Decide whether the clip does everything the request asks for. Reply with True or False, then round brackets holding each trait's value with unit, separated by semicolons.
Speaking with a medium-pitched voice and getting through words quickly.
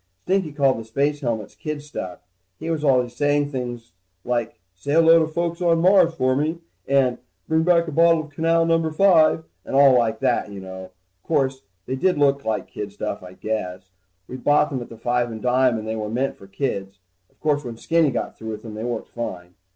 False (130 Hz; 215 wpm)